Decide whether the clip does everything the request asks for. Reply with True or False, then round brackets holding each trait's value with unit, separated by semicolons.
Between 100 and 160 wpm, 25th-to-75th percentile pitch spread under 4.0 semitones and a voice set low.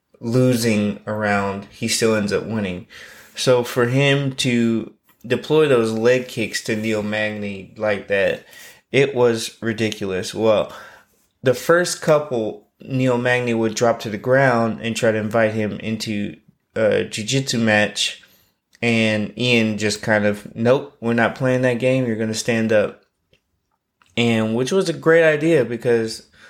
True (145 wpm; 2.7 semitones; 115 Hz)